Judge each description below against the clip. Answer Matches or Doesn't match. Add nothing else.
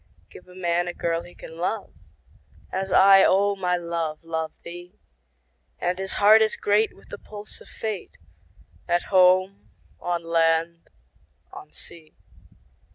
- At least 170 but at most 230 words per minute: Doesn't match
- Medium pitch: Matches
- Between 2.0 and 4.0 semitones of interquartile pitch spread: Matches